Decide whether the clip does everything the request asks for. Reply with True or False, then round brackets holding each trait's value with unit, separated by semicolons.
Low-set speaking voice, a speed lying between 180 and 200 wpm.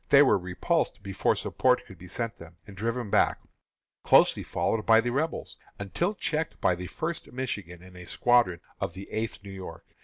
True (100 Hz; 185 wpm)